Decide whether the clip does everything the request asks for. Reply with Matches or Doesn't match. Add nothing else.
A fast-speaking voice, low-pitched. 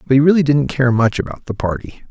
Matches